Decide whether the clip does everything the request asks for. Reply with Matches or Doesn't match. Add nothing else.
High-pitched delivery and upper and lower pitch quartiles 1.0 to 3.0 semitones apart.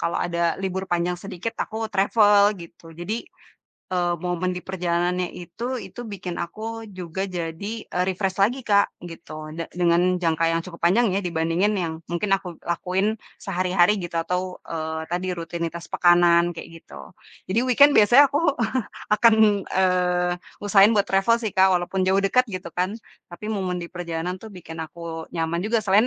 Doesn't match